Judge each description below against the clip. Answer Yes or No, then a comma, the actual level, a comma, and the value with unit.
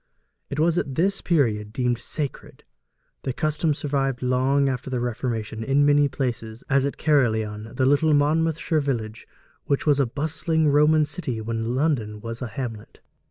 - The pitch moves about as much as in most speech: Yes, average, 4.4 semitones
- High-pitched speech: No, low, 135 Hz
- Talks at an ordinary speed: Yes, average, 160 wpm